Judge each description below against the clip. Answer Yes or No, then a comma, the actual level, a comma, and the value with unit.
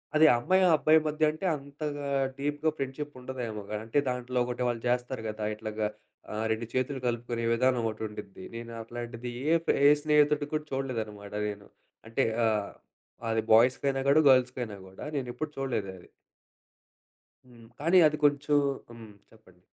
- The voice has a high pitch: No, low, 125 Hz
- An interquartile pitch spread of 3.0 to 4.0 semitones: No, average, 4.4 semitones